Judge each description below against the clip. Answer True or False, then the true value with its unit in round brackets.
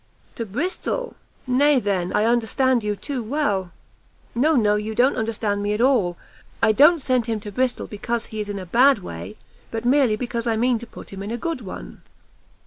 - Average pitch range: True (3.8 semitones)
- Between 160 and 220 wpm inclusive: True (200 wpm)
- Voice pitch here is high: True (230 Hz)